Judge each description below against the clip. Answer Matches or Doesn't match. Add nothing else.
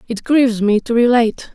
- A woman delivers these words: Matches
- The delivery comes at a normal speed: Matches